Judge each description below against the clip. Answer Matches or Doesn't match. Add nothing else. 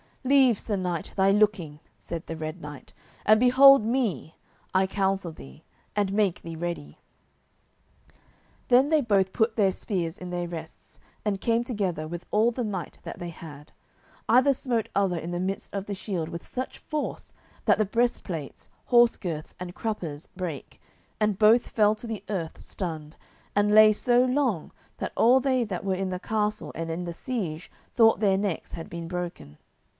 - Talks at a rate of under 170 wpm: Doesn't match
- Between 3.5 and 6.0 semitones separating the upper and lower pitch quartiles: Matches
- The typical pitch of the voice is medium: Doesn't match